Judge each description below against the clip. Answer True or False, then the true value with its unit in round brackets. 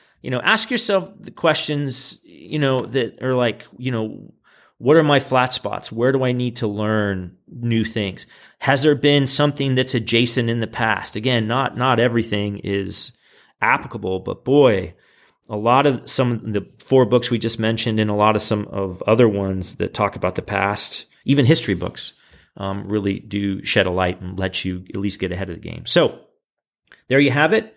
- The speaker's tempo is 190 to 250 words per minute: True (195 wpm)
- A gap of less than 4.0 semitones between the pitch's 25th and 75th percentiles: False (4.8 semitones)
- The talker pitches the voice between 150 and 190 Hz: False (115 Hz)